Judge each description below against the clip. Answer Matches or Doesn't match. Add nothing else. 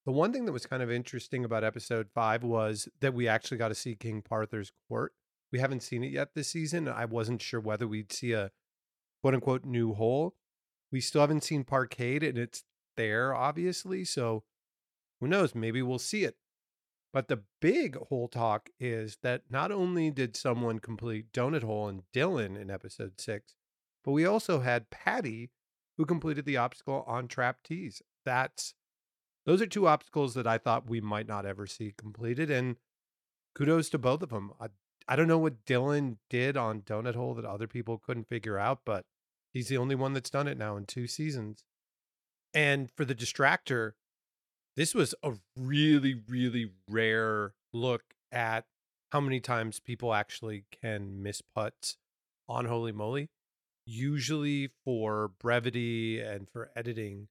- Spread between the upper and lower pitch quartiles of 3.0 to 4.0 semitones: Matches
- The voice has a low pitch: Matches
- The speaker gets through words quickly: Doesn't match